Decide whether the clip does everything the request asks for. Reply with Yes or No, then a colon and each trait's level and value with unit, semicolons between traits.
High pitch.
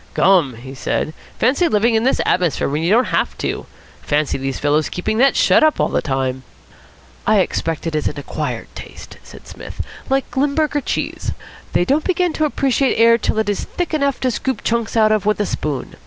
Yes: high, 220 Hz